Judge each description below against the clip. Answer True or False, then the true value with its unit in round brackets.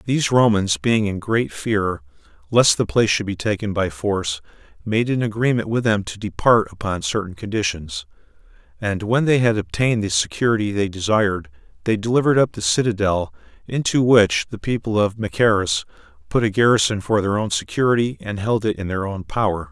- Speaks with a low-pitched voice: True (105 Hz)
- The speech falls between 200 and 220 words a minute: False (175 wpm)